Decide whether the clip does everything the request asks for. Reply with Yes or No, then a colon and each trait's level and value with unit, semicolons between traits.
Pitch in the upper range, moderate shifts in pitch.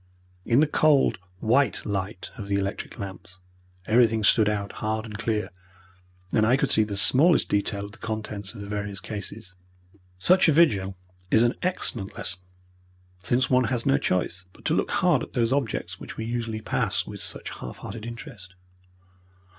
No: low, 110 Hz; average, 3.3 semitones